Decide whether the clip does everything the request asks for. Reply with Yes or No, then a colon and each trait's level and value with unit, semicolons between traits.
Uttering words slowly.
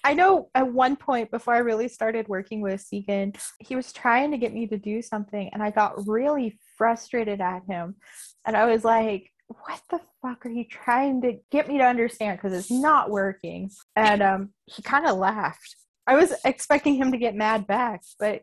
No: average, 200 wpm